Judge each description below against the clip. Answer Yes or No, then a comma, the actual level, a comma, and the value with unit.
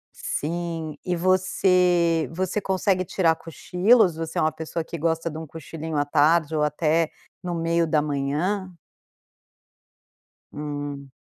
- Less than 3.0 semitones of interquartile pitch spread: Yes, narrow, 2.6 semitones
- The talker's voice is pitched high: No, medium, 165 Hz